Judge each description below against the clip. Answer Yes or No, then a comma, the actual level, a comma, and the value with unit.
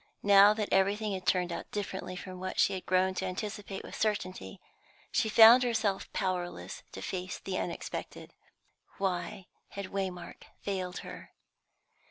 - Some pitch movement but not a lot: No, narrow, 1.9 semitones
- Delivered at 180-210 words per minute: No, average, 145 wpm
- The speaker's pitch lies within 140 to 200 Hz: Yes, high, 190 Hz